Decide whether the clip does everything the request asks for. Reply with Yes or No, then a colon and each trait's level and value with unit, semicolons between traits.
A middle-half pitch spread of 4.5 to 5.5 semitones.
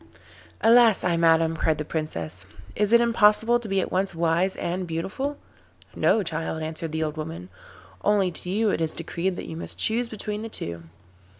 Yes: average, 4.8 semitones